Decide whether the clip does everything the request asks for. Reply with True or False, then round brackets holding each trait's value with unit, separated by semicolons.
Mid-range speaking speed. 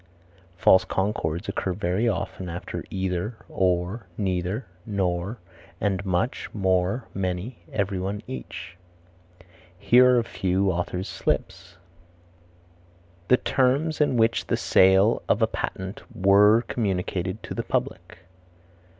False (115 wpm)